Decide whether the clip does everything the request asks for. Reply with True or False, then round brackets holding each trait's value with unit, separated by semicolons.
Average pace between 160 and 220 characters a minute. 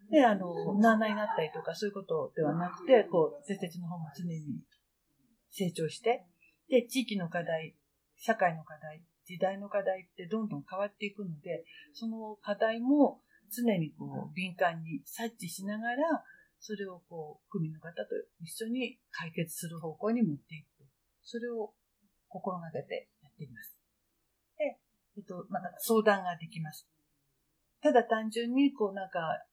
False (295 characters per minute)